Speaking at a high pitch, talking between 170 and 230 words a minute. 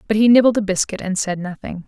No: high, 205 Hz; fast, 255 wpm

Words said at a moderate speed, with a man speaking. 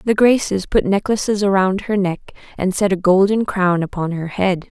No: average, 190 wpm; female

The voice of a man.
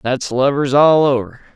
Yes: male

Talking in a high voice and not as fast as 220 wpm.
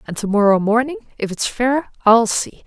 Yes: high, 230 Hz; fast, 205 wpm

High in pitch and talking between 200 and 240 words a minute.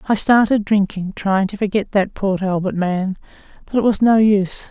No: high, 200 Hz; average, 190 wpm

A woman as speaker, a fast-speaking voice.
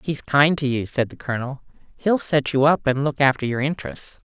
Yes: female; fast, 225 wpm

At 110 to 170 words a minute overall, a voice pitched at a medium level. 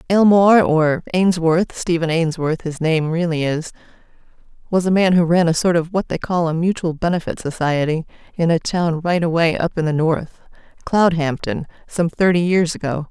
Yes: average, 165 wpm; medium, 170 Hz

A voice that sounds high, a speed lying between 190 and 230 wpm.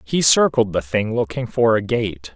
No: low, 110 Hz; fast, 205 wpm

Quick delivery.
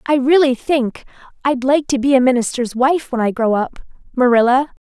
No: average, 180 wpm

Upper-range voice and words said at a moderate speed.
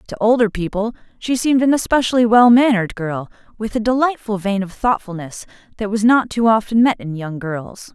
Yes: high, 215 Hz; average, 190 wpm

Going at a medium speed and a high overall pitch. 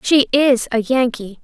Yes: average, 165 wpm; very high, 250 Hz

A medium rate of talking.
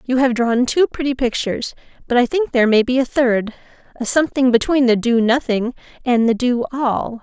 Yes: average, 190 wpm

